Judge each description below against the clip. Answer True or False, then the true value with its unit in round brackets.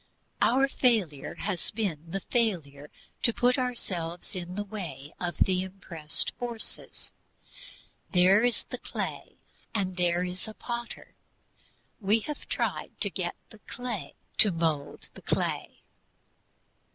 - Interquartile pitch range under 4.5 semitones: False (4.9 semitones)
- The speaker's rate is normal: False (130 wpm)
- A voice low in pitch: False (190 Hz)